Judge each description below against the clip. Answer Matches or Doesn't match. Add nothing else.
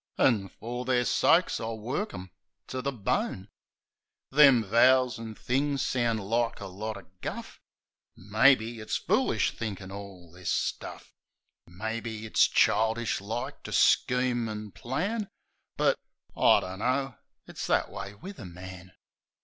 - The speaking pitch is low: Matches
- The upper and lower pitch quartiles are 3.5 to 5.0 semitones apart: Matches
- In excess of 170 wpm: Doesn't match